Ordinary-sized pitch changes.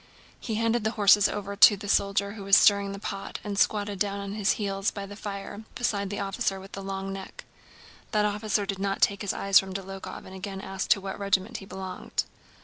No: narrow, 1.0 semitones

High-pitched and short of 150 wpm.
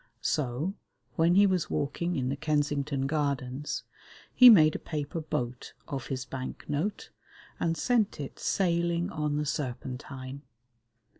No: medium, 150 Hz; slow, 135 wpm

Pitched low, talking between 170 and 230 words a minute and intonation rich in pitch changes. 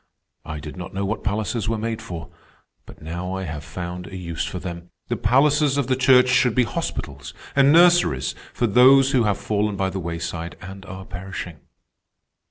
Yes: very low, 95 Hz; average, 185 wpm; wide, 6.3 semitones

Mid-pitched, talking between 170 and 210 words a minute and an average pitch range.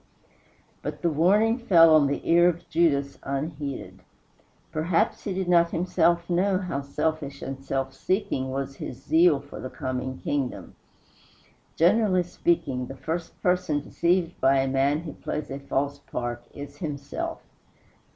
No: medium, 155 Hz; average, 145 wpm; average, 4.0 semitones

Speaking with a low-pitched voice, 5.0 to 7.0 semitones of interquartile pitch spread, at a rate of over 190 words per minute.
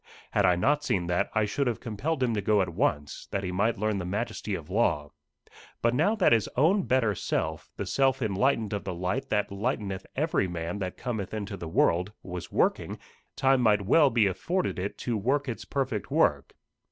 Yes: low, 105 Hz; wide, 5.6 semitones; average, 200 wpm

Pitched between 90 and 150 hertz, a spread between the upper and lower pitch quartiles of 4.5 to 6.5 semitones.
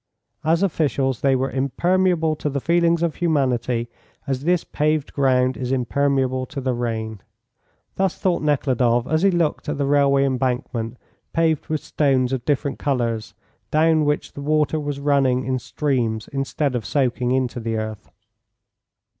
No: medium, 140 Hz; average, 3.3 semitones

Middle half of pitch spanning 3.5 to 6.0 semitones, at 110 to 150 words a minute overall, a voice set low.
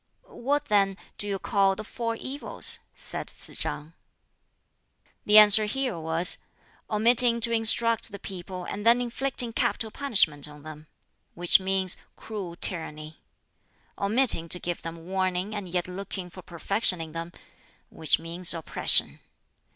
No: average, 4.7 semitones; average, 140 wpm; high, 195 Hz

